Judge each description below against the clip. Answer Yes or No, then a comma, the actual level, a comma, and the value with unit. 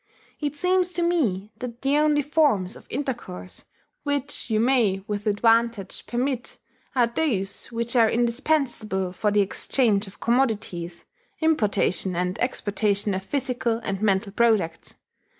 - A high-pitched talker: Yes, high, 230 Hz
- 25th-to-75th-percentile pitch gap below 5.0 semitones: No, average, 5.3 semitones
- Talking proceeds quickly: No, slow, 135 wpm